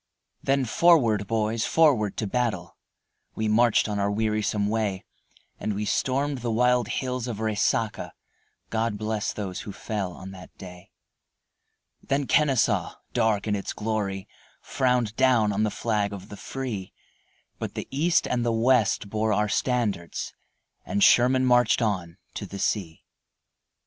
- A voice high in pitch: No, low, 110 Hz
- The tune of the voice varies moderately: Yes, average, 3.2 semitones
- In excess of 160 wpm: No, average, 145 wpm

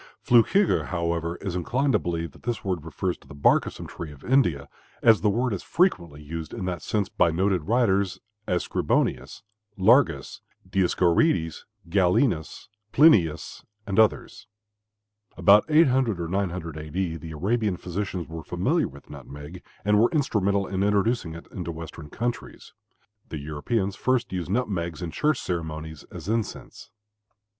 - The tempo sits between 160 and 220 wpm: No, average, 150 wpm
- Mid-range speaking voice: No, very low, 90 Hz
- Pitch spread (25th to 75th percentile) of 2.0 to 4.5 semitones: No, average, 5.0 semitones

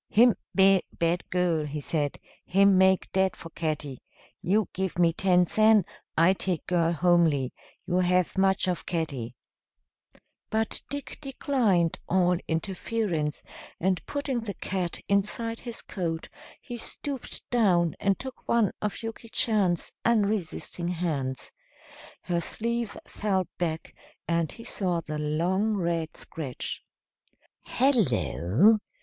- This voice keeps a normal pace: No, slow, 125 wpm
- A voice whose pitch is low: No, medium, 180 Hz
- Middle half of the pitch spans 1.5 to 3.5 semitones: No, average, 4.3 semitones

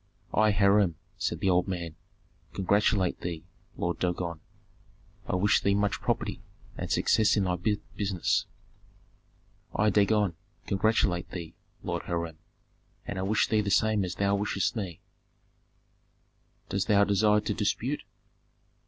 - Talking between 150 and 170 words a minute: No, slow, 135 wpm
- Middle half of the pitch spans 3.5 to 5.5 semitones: No, average, 2.8 semitones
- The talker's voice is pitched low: Yes, low, 100 Hz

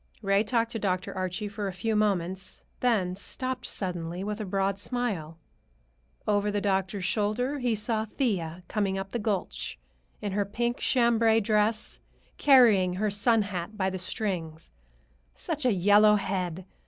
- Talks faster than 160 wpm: No, average, 155 wpm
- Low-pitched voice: No, high, 205 Hz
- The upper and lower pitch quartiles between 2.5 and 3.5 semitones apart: Yes, average, 3.0 semitones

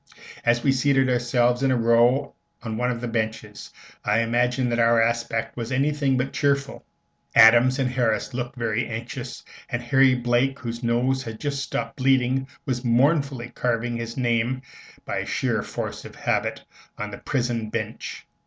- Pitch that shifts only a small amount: Yes, narrow, 2.1 semitones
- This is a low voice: Yes, low, 120 Hz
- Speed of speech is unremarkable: Yes, average, 165 wpm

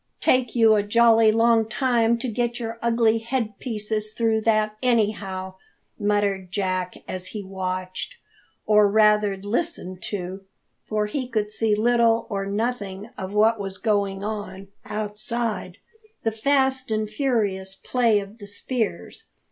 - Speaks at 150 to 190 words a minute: No, average, 140 wpm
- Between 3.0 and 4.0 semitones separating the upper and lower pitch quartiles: No, narrow, 2.6 semitones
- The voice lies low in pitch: No, high, 215 Hz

